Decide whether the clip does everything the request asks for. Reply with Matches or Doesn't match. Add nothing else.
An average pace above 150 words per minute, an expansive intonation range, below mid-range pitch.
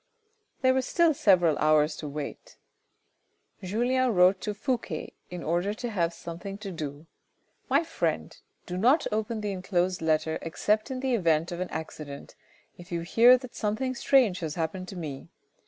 Doesn't match